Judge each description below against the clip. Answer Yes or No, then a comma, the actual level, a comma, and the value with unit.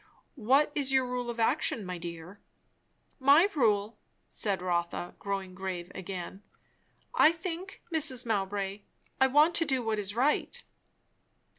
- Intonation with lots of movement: Yes, wide, 6.3 semitones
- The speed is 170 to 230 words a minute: No, slow, 135 wpm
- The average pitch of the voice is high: Yes, high, 225 Hz